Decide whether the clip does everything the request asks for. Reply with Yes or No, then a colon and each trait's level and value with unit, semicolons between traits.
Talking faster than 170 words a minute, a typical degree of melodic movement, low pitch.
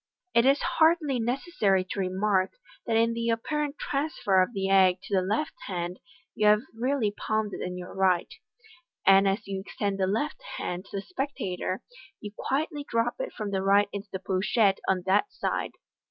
No: average, 185 wpm; average, 4.0 semitones; high, 205 Hz